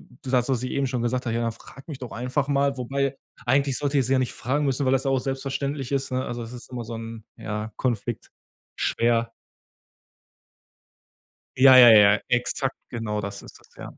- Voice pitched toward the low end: Yes, low, 125 Hz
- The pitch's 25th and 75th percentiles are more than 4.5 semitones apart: No, average, 2.7 semitones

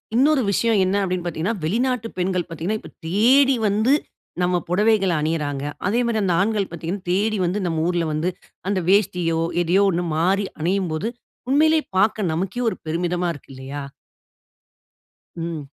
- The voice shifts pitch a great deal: No, average, 4.3 semitones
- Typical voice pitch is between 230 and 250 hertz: No, medium, 185 Hz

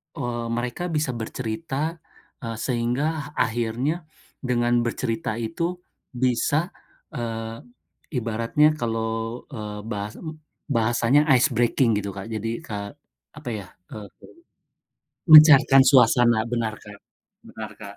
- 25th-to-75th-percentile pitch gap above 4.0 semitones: No, average, 3.3 semitones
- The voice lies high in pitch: No, low, 120 Hz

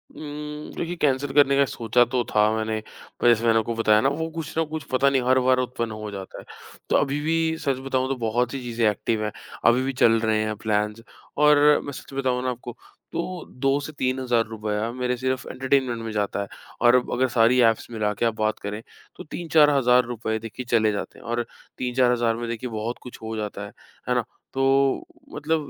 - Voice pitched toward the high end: No, low, 125 Hz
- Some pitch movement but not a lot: Yes, average, 3.4 semitones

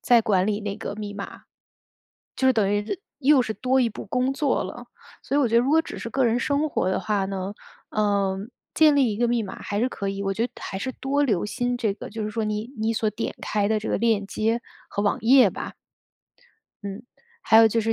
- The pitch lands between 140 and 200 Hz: No, high, 220 Hz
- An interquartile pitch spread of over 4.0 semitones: No, average, 3.4 semitones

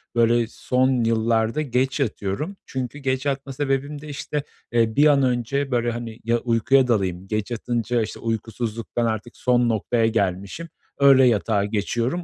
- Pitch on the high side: No, low, 120 Hz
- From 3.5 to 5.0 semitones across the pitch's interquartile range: No, average, 3.1 semitones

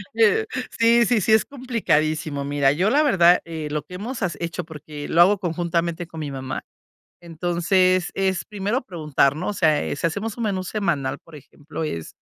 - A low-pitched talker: No, medium, 170 Hz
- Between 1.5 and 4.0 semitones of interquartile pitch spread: No, average, 4.9 semitones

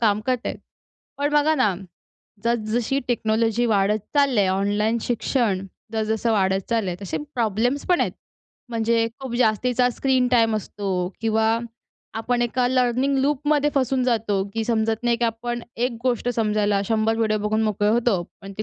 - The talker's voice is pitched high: Yes, high, 230 Hz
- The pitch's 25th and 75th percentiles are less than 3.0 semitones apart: Yes, narrow, 2.5 semitones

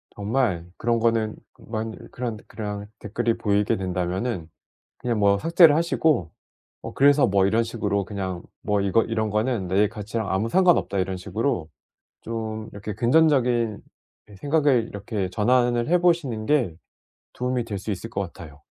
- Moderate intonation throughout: Yes, average, 3.5 semitones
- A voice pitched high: No, low, 110 Hz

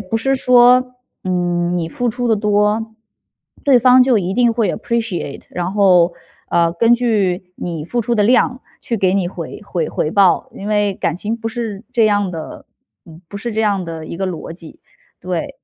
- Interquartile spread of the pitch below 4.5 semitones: No, average, 4.8 semitones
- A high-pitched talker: Yes, high, 205 Hz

